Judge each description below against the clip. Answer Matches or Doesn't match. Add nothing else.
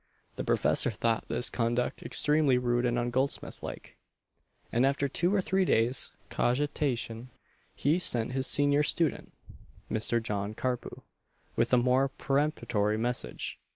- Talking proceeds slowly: Matches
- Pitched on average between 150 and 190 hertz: Doesn't match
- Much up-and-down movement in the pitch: Doesn't match